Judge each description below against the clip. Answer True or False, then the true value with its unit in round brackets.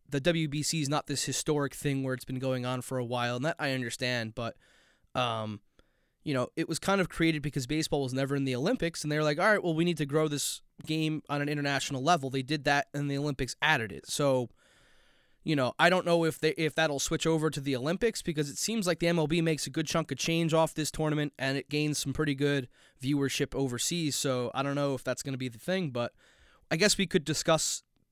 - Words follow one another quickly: True (245 wpm)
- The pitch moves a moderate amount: True (3.1 semitones)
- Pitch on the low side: False (150 Hz)